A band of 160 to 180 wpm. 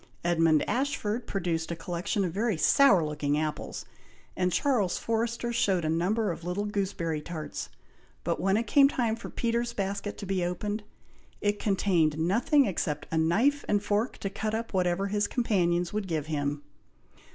Yes: average, 165 wpm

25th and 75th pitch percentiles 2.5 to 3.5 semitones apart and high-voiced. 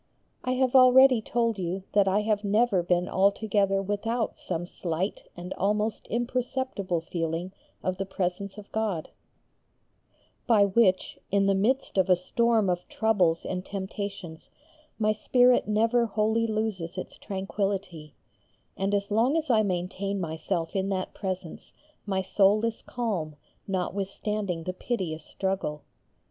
Yes: average, 3.2 semitones; high, 200 Hz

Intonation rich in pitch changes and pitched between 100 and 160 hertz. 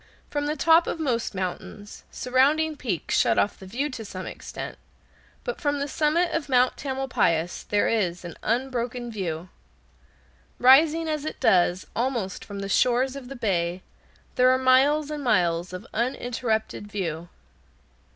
No: wide, 6.5 semitones; high, 245 Hz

